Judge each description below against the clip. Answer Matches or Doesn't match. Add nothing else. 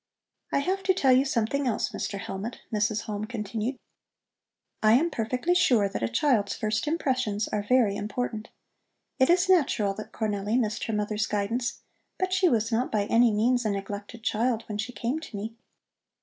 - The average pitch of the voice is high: Matches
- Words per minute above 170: Matches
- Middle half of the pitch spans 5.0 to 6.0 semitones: Doesn't match